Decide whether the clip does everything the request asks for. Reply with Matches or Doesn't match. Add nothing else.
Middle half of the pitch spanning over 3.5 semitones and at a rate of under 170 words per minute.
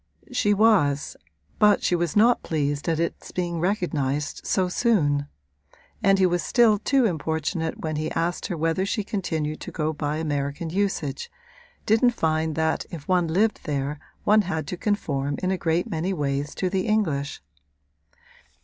Matches